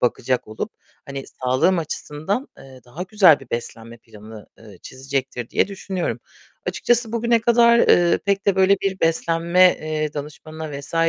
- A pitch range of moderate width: No, wide, 6.7 semitones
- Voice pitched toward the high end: No, medium, 155 Hz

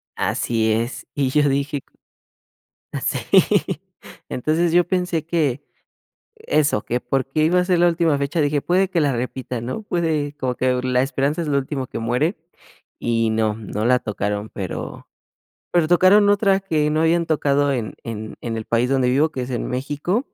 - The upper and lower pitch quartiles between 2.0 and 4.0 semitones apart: No, average, 5.1 semitones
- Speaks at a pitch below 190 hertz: Yes, medium, 140 Hz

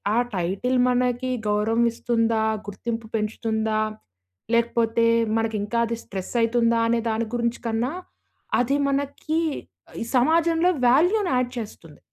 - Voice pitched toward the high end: Yes, high, 235 Hz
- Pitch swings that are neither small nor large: No, narrow, 2.1 semitones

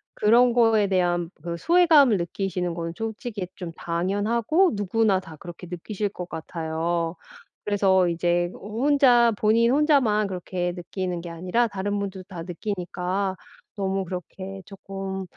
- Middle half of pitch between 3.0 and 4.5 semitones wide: Yes, average, 3.7 semitones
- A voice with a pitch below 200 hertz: Yes, high, 190 Hz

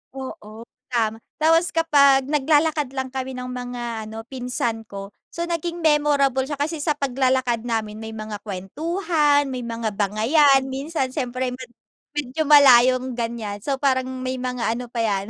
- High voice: Yes, very high, 255 Hz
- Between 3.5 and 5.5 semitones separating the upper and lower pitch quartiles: Yes, average, 4.0 semitones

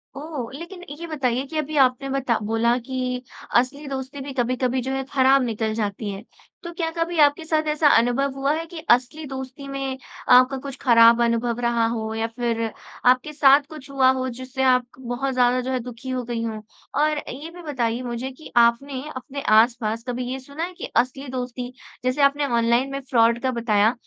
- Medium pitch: No, very high, 255 Hz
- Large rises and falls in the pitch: No, average, 2.8 semitones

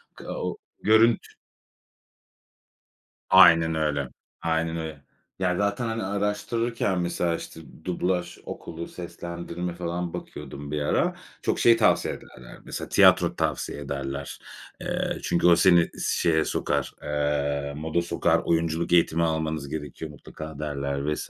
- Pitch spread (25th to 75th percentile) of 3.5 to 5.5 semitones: No, average, 3.1 semitones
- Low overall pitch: Yes, very low, 80 Hz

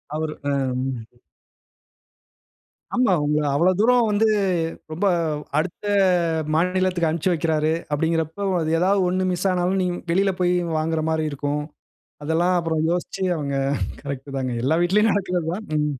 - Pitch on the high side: No, medium, 170 Hz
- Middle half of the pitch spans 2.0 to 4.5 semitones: Yes, average, 3.3 semitones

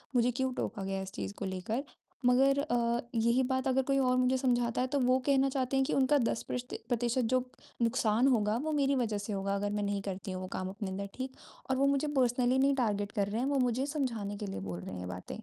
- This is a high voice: Yes, high, 245 Hz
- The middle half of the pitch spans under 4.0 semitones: No, average, 4.5 semitones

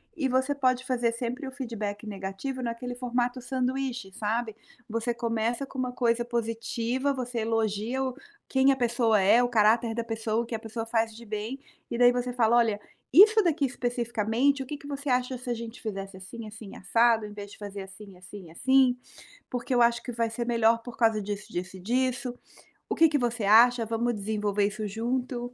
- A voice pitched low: No, high, 235 Hz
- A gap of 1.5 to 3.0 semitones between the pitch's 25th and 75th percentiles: Yes, narrow, 2.5 semitones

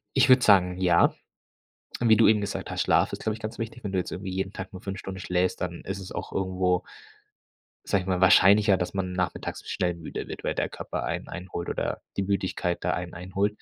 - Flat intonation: Yes, narrow, 2.0 semitones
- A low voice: Yes, very low, 95 Hz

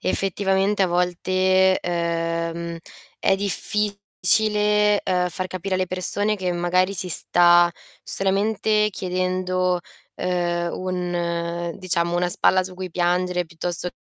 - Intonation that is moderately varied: No, narrow, 1.7 semitones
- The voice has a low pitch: No, medium, 185 Hz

